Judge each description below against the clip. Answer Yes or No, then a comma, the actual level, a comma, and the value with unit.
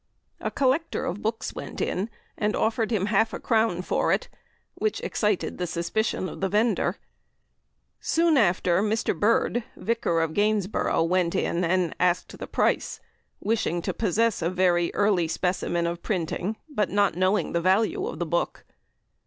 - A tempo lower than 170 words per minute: Yes, average, 155 wpm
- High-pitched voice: Yes, high, 200 Hz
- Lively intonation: No, average, 4.0 semitones